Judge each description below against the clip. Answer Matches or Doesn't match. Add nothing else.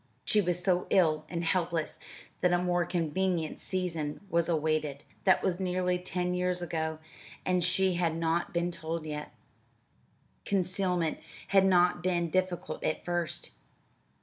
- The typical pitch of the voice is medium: Matches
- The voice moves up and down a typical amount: Doesn't match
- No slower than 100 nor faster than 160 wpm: Matches